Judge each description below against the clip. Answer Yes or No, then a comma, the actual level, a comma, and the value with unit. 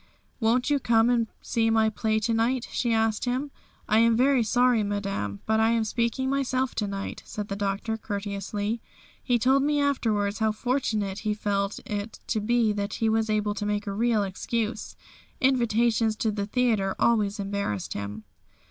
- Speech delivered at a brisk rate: No, average, 175 wpm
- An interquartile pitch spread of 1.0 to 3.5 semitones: Yes, average, 2.7 semitones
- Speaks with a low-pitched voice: No, high, 220 Hz